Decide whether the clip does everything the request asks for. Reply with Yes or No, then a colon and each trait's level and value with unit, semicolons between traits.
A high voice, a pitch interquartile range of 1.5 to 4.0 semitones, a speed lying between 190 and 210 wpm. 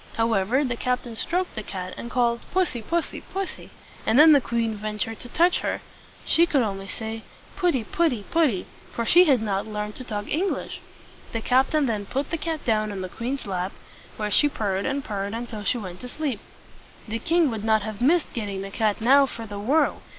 No: high, 230 Hz; average, 5.1 semitones; average, 200 wpm